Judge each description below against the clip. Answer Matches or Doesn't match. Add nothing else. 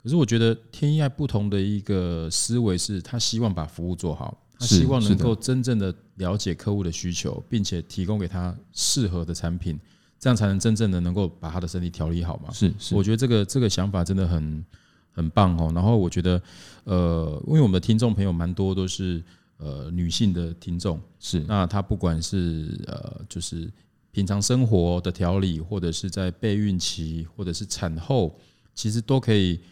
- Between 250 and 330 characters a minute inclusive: Matches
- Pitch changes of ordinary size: Matches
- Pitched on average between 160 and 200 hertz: Doesn't match